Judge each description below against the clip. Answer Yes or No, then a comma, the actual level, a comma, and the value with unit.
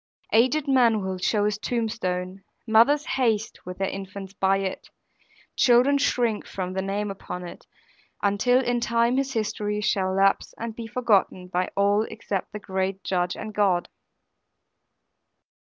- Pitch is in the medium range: No, high, 205 Hz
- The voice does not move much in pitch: No, average, 3.5 semitones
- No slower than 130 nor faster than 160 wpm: Yes, average, 145 wpm